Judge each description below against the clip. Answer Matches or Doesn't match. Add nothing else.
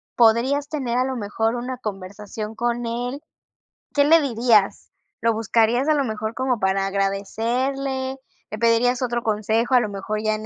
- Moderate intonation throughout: Matches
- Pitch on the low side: Doesn't match